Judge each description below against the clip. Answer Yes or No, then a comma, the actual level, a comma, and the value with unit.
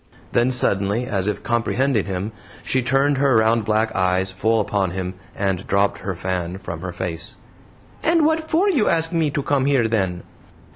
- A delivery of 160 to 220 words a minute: Yes, average, 180 wpm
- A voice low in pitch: Yes, low, 110 Hz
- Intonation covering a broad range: Yes, wide, 6.3 semitones